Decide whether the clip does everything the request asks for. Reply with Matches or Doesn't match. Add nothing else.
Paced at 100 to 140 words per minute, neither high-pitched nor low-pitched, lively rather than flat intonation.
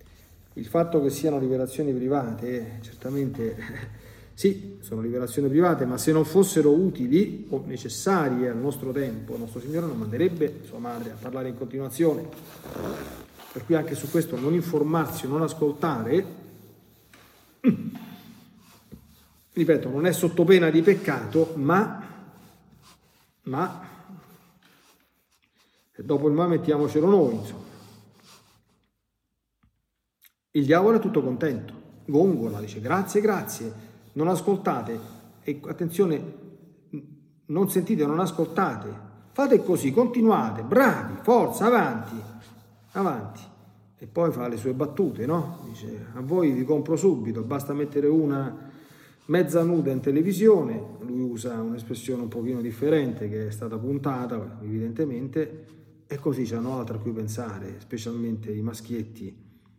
Matches